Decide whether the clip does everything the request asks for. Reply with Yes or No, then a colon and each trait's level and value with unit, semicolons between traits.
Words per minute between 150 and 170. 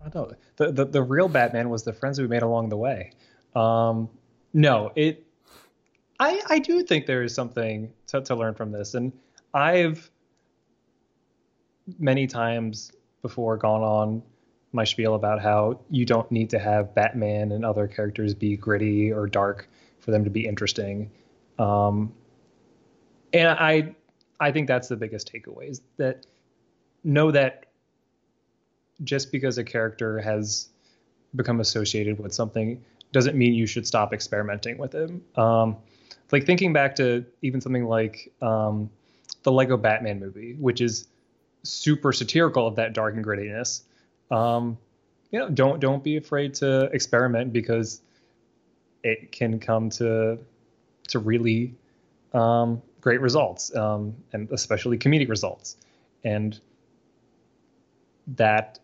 No: average, 140 wpm